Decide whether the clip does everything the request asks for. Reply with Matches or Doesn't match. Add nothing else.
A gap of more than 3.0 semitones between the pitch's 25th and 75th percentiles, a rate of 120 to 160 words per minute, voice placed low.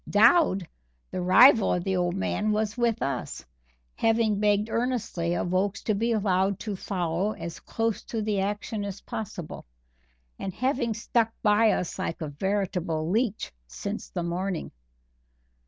Doesn't match